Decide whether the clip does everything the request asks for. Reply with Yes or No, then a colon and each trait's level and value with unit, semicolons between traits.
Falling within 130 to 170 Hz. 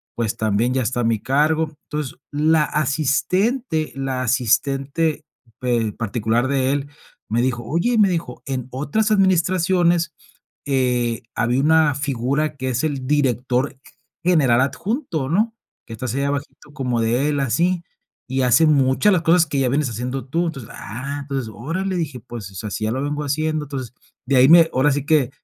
Yes: medium, 140 Hz